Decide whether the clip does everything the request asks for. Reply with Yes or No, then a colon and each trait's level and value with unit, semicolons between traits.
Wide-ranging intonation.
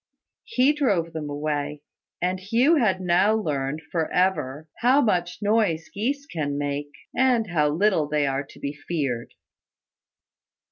Yes: wide, 6.6 semitones